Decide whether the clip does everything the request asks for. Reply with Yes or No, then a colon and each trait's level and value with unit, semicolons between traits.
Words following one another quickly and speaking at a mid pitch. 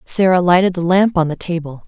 Yes: fast, 225 wpm; medium, 175 Hz